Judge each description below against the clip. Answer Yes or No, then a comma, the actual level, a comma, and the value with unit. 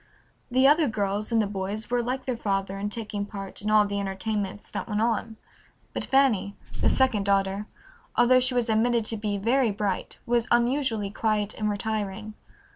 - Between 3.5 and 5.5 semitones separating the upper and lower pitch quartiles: No, average, 2.9 semitones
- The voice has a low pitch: No, high, 215 Hz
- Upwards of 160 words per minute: Yes, average, 180 wpm